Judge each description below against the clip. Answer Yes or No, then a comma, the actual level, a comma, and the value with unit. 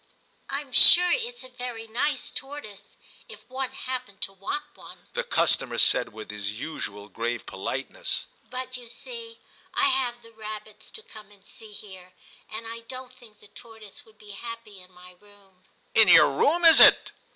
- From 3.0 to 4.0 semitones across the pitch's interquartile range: No, average, 4.9 semitones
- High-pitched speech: Yes, high, 225 Hz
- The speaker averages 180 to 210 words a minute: Yes, average, 190 wpm